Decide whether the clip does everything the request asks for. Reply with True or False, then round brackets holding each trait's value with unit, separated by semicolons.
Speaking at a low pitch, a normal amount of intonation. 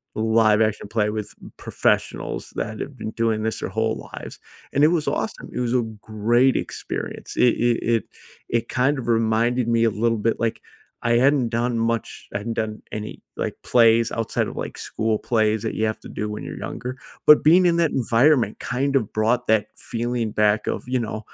False (115 Hz; 2.2 semitones)